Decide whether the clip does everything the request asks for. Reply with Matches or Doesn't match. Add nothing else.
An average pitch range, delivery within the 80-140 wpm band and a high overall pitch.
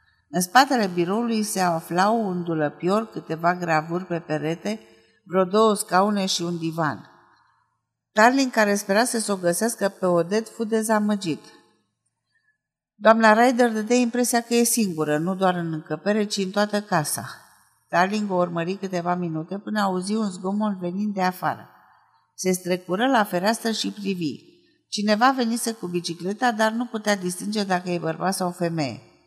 Doesn't match